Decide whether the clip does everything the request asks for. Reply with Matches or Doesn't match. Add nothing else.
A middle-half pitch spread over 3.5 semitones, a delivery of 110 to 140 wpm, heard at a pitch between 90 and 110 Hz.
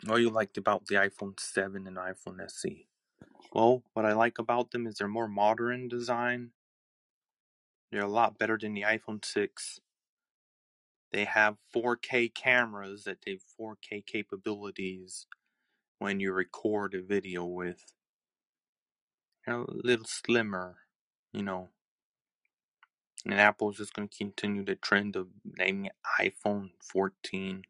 Doesn't match